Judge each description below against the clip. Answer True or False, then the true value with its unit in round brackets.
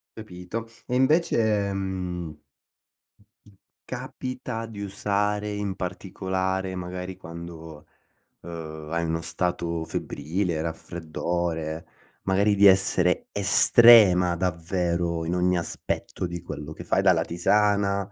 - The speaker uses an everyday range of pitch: True (3.1 semitones)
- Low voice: True (90 Hz)